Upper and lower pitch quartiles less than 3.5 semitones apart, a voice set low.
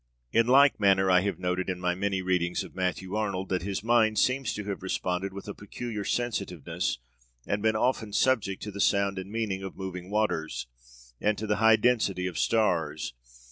Yes: average, 2.8 semitones; low, 100 Hz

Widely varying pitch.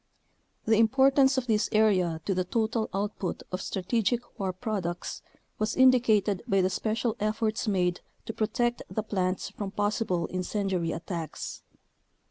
No: average, 3.4 semitones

